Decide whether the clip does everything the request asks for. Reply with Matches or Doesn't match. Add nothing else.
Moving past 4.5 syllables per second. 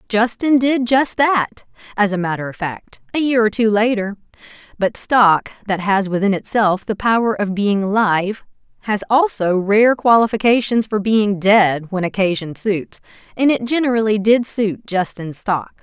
Doesn't match